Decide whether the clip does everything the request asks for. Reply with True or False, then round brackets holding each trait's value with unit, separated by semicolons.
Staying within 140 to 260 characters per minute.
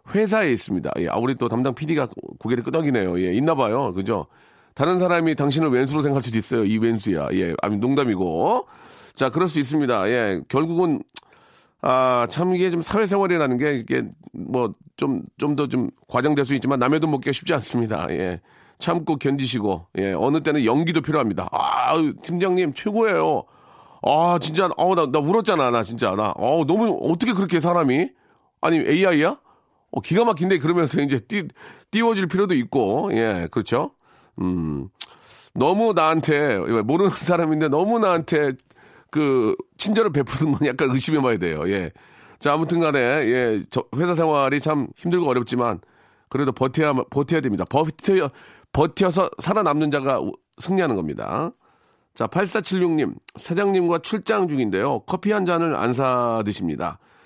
False (325 characters per minute)